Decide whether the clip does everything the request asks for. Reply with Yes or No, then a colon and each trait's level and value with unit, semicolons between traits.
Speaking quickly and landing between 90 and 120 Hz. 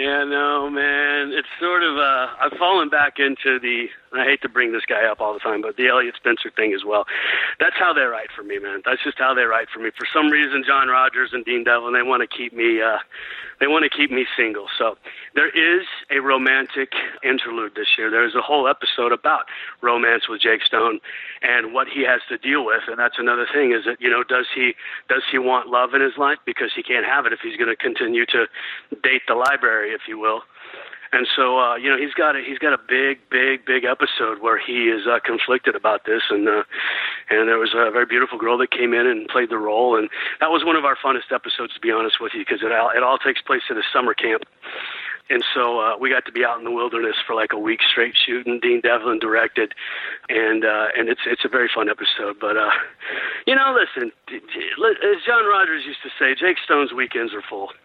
No: fast, 240 wpm; medium, 140 Hz